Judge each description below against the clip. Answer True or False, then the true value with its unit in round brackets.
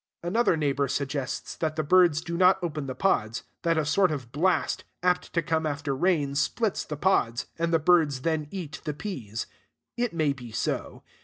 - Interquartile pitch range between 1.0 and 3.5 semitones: False (3.9 semitones)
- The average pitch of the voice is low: False (155 Hz)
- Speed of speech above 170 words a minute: True (185 wpm)